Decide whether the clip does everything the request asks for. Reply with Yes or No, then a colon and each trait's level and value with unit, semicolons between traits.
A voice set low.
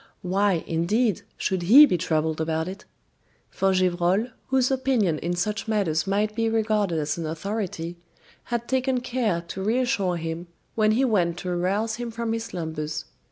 No: high, 195 Hz